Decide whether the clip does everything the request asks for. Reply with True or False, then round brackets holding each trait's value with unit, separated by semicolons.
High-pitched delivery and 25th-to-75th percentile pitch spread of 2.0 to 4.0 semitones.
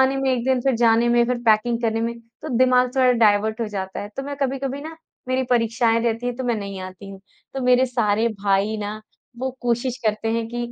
True (235 Hz; 2.9 semitones)